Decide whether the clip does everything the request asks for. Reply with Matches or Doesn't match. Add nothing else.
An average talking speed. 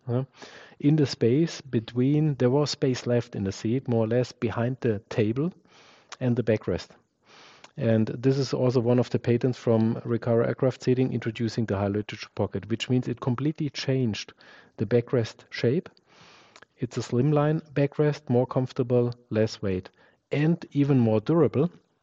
Matches